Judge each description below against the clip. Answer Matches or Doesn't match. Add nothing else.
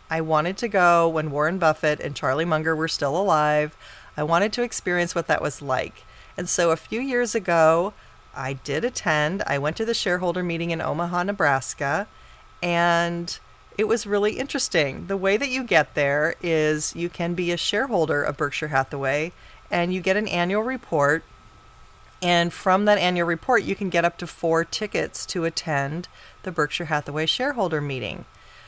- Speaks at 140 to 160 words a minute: Doesn't match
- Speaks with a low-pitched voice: Doesn't match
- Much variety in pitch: Doesn't match